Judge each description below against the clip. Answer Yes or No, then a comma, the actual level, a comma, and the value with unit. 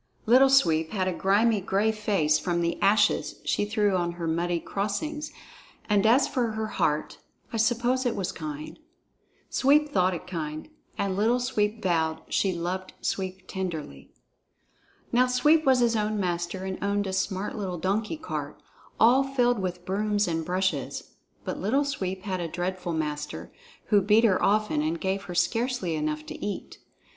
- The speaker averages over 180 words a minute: No, average, 165 wpm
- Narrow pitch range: No, average, 4.2 semitones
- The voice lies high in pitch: Yes, high, 195 Hz